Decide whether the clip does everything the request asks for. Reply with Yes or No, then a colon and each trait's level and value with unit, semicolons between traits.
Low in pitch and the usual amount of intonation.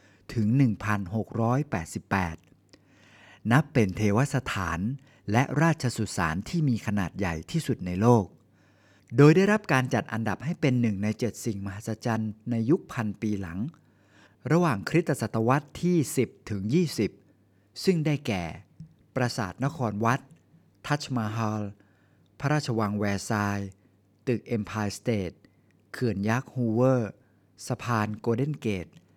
Yes: low, 110 Hz; average, 4.3 semitones